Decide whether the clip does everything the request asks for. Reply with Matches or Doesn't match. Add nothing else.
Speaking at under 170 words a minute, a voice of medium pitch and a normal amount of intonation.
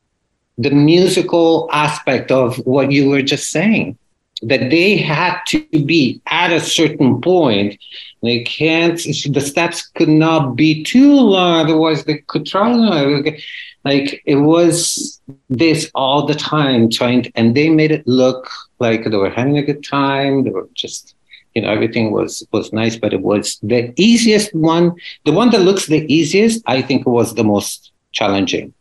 Matches